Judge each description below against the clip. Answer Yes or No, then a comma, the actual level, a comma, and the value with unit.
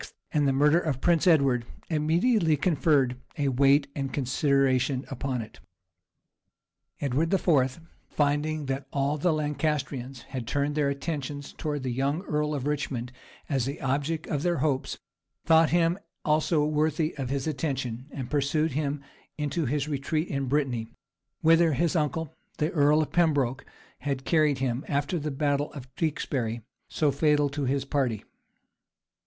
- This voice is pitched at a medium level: Yes, medium, 145 Hz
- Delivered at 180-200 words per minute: No, average, 150 wpm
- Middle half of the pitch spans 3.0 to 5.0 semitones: No, narrow, 2.4 semitones